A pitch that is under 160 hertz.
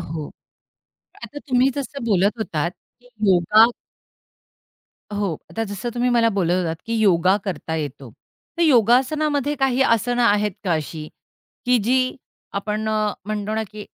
No: high, 215 Hz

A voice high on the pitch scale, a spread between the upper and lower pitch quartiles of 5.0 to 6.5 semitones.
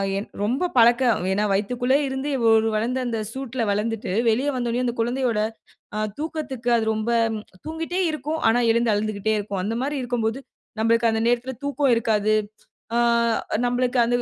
No: high, 235 Hz; average, 3.1 semitones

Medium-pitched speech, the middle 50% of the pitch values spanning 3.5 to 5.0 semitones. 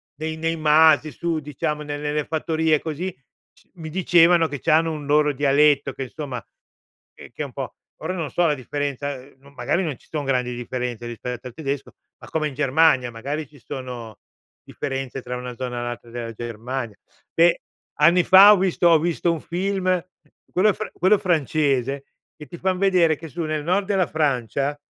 Yes: medium, 150 Hz; average, 4.0 semitones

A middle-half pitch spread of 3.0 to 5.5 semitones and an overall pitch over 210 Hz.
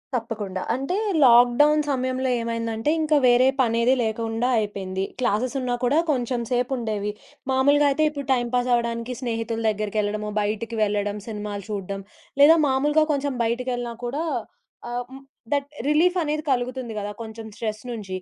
Yes: average, 3.3 semitones; high, 240 Hz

